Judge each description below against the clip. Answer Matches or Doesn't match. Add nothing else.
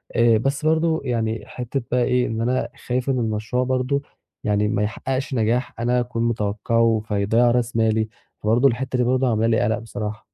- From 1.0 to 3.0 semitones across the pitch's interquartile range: Matches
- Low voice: Matches